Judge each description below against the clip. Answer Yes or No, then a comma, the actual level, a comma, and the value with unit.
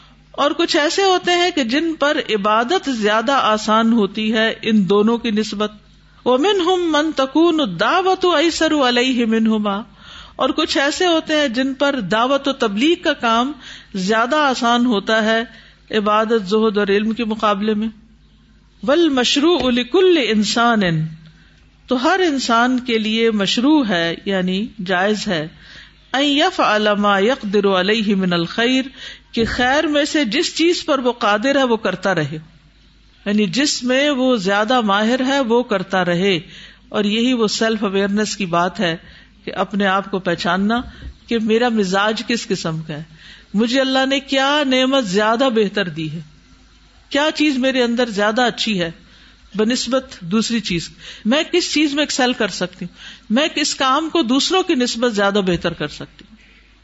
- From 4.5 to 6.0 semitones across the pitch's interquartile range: Yes, average, 5.1 semitones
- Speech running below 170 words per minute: Yes, average, 160 wpm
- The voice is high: Yes, high, 230 Hz